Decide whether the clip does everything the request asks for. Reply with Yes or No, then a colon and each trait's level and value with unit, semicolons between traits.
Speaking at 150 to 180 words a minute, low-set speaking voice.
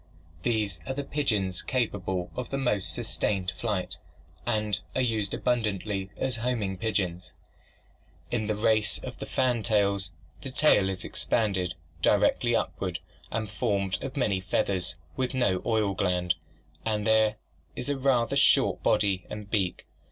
No: slow, 135 wpm; low, 105 Hz